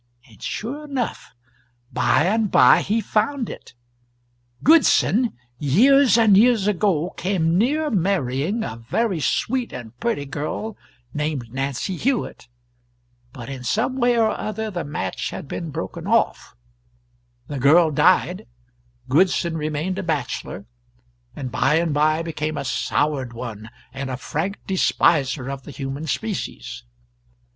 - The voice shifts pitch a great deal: Yes, wide, 7.9 semitones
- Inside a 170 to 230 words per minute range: No, slow, 135 wpm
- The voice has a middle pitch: Yes, medium, 165 Hz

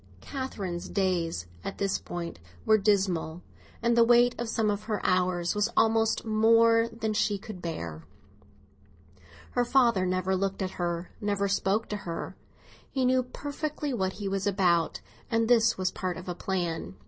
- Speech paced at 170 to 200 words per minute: No, average, 160 wpm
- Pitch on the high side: Yes, high, 200 Hz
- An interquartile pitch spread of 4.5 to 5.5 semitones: No, average, 3.8 semitones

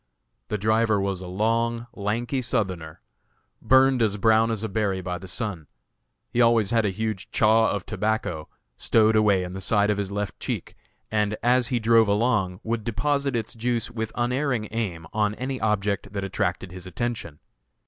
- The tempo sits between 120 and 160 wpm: No, average, 175 wpm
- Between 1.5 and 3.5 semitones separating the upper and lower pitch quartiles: Yes, average, 2.9 semitones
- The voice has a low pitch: Yes, low, 110 Hz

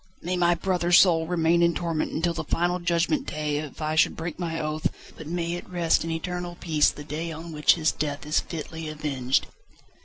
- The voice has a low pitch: No, medium, 165 Hz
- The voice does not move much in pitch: Yes, narrow, 2.1 semitones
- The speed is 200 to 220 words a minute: Yes, fast, 205 wpm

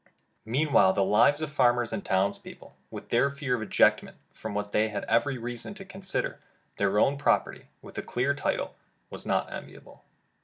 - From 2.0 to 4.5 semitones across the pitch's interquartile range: No, average, 5.2 semitones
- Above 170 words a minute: Yes, average, 180 wpm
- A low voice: Yes, low, 120 Hz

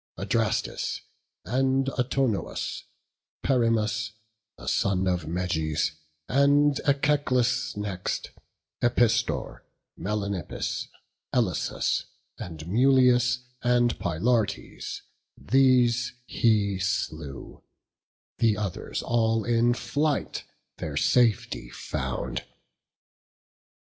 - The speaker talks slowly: Yes, slow, 75 wpm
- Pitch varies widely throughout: No, average, 4.4 semitones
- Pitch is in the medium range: No, low, 115 Hz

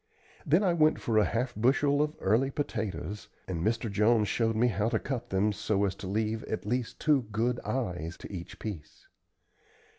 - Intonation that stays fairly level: No, average, 3.7 semitones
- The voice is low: Yes, low, 110 Hz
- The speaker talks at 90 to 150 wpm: No, average, 185 wpm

